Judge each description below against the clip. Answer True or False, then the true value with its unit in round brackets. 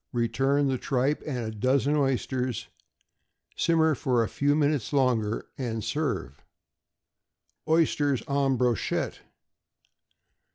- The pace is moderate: False (100 wpm)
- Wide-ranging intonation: False (3.3 semitones)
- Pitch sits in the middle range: False (130 Hz)